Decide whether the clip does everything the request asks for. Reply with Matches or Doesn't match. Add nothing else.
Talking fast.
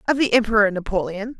Doesn't match